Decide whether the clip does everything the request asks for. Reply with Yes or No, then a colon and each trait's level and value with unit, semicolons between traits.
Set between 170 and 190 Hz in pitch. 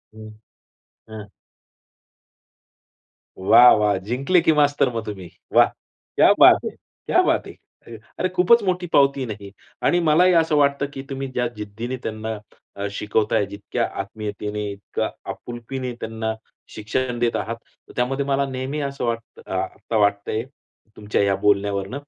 No: low, 115 Hz